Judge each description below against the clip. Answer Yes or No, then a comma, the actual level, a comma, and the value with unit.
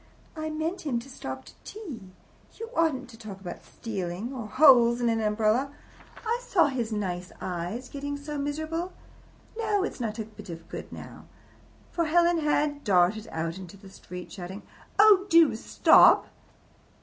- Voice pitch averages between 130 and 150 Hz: No, high, 245 Hz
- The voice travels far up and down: Yes, wide, 7.7 semitones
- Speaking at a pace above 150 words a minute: Yes, average, 160 wpm